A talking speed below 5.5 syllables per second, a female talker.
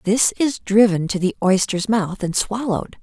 Yes: 4.6 syllables/s; female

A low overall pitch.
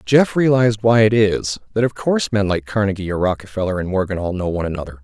Yes: low, 100 Hz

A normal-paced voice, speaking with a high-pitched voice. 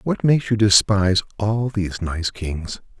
No: average, 160 wpm; low, 100 Hz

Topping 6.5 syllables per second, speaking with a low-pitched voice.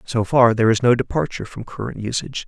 Yes: 6.8 syllables/s; low, 120 Hz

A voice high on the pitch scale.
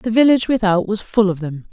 Yes: high, 205 Hz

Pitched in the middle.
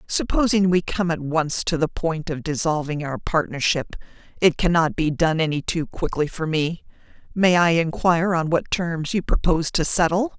Yes: medium, 165 Hz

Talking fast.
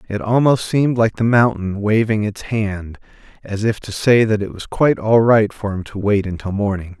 Yes: fast, 215 wpm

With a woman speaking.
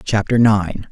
No: male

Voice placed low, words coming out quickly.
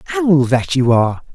No: low, 130 Hz; average, 180 wpm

